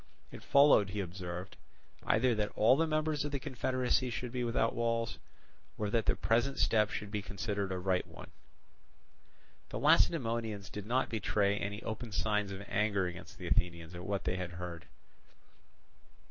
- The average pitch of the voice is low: Yes, low, 105 Hz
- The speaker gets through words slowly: No, average, 160 wpm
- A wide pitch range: No, average, 3.6 semitones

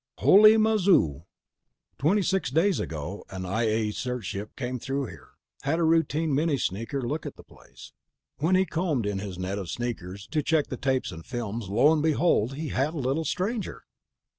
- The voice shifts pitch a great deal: Yes, wide, 7.4 semitones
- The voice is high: No, low, 135 Hz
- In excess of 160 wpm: Yes, average, 190 wpm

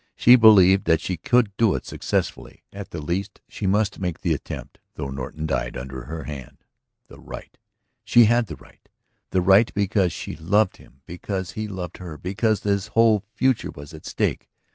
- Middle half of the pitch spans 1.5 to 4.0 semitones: No, average, 4.9 semitones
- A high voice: No, very low, 95 Hz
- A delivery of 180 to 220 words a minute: Yes, average, 185 wpm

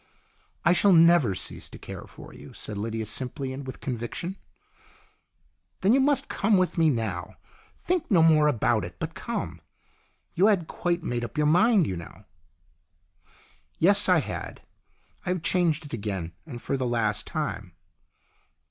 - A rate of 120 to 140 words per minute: No, average, 165 wpm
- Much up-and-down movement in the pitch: Yes, wide, 7.9 semitones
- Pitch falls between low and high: Yes, medium, 150 Hz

